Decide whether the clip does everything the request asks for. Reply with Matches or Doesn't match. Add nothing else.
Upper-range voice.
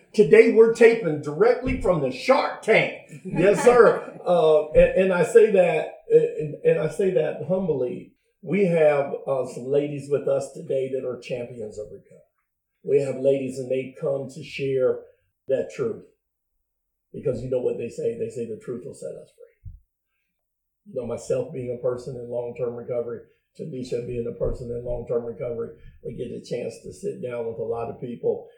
Matches